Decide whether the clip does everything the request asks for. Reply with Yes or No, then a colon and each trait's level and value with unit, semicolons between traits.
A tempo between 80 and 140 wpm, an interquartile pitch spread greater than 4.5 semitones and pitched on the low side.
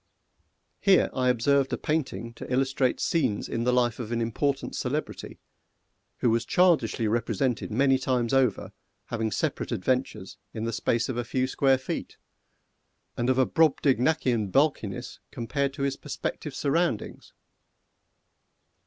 No: slow, 135 wpm; average, 2.9 semitones; low, 130 Hz